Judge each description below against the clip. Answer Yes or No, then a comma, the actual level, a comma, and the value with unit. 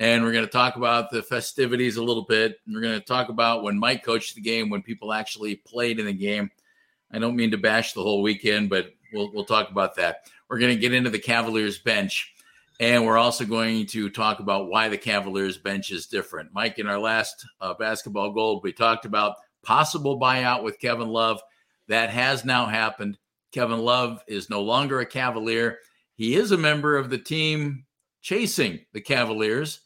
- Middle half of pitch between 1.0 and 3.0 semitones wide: Yes, narrow, 2.5 semitones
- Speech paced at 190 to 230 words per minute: Yes, average, 200 wpm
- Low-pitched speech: Yes, low, 115 Hz